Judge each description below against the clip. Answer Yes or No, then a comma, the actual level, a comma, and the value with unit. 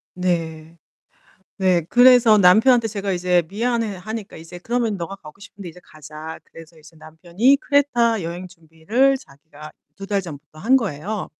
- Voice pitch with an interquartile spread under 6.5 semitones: Yes, wide, 5.6 semitones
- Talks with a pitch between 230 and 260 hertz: No, medium, 185 Hz